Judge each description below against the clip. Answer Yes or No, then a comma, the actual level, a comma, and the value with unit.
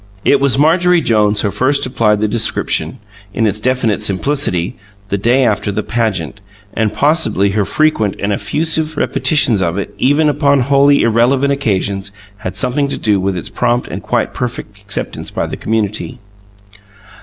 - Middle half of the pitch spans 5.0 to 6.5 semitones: Yes, wide, 5.4 semitones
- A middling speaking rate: Yes, average, 160 wpm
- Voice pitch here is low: Yes, low, 115 Hz